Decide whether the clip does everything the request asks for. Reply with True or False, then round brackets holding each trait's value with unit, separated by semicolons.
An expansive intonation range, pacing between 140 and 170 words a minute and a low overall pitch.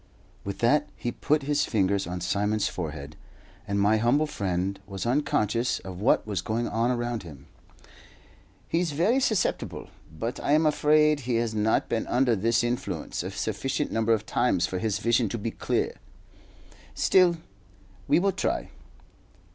True (6.0 semitones; 155 wpm; 115 Hz)